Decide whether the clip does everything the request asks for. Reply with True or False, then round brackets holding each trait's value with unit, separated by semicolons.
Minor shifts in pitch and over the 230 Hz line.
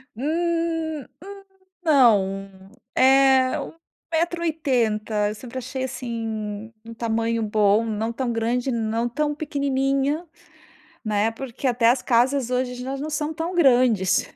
False (4.2 semitones; 250 Hz)